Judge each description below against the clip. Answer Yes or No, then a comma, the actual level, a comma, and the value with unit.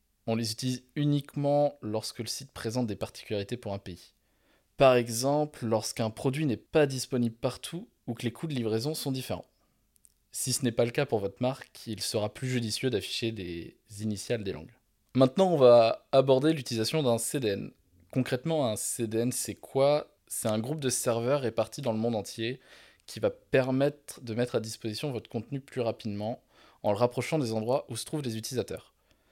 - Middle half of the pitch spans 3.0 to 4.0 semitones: Yes, average, 3.5 semitones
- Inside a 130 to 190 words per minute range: Yes, average, 185 wpm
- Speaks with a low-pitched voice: Yes, low, 120 Hz